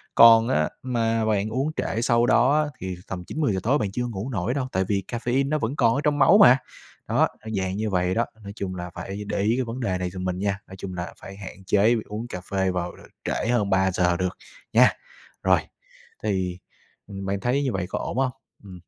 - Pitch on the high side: No, low, 105 Hz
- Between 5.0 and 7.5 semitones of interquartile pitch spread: No, average, 4.4 semitones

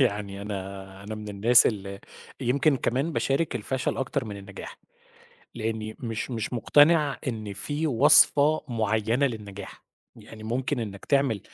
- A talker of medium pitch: No, low, 115 Hz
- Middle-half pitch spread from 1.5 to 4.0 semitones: No, average, 4.6 semitones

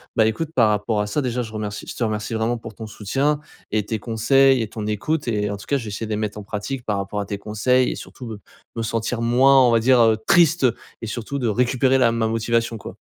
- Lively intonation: No, average, 2.9 semitones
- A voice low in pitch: Yes, low, 115 Hz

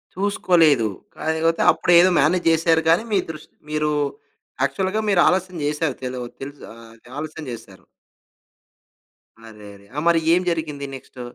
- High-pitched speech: No, medium, 160 Hz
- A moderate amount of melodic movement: Yes, average, 4.0 semitones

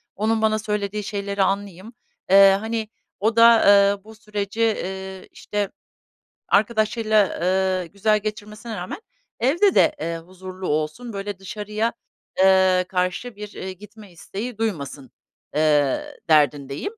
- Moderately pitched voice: No, high, 200 Hz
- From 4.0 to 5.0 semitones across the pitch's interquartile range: No, average, 2.7 semitones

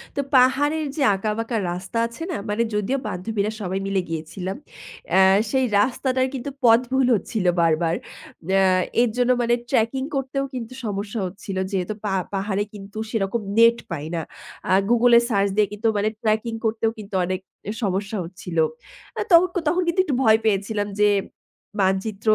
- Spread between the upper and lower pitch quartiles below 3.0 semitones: No, average, 3.8 semitones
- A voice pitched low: No, high, 215 Hz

